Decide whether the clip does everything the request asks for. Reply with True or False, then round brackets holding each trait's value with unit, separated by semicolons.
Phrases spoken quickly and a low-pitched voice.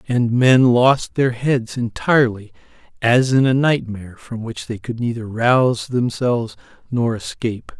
False (145 wpm; 120 Hz)